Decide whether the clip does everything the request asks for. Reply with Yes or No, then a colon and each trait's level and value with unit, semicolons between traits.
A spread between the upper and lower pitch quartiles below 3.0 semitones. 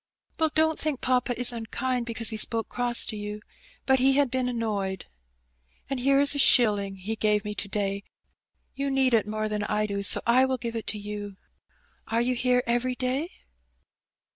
No: average, 3.4 semitones